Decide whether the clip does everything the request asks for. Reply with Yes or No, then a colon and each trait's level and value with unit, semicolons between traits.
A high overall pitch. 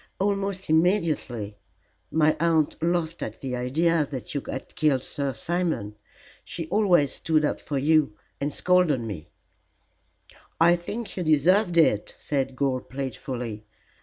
No: medium, 155 Hz